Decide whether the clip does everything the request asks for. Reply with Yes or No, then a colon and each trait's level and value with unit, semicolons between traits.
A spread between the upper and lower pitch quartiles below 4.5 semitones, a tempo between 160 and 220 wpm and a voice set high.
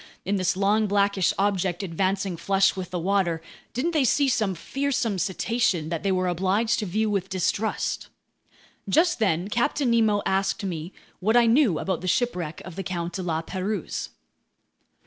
Yes: average, 3.3 semitones; average, 165 wpm; high, 195 Hz